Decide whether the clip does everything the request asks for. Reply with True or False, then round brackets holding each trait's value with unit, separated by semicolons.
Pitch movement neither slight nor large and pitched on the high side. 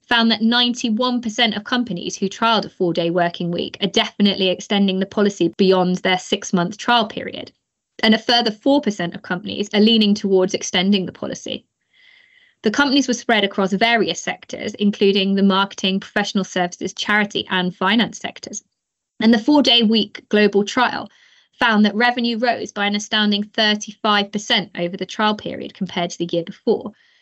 True (3.4 semitones; 210 Hz)